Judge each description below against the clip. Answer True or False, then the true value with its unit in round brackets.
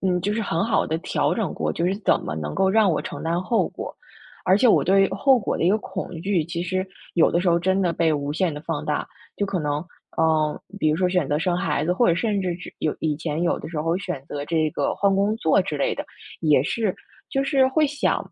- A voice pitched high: False (175 Hz)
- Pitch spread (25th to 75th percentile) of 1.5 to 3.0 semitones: False (3.8 semitones)